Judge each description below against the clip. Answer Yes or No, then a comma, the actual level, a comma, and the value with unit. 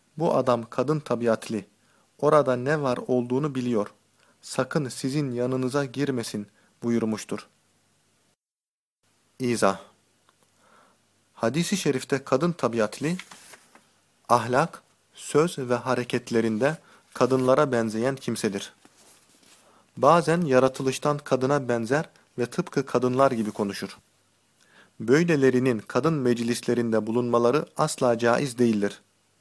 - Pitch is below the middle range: Yes, low, 125 Hz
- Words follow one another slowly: Yes, slow, 85 wpm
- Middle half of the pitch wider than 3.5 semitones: No, average, 3.2 semitones